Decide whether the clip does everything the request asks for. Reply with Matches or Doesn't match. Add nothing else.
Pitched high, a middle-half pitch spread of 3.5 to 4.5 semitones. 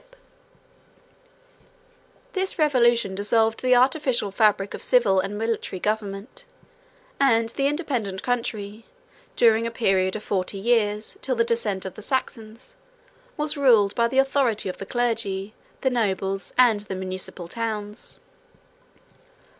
Matches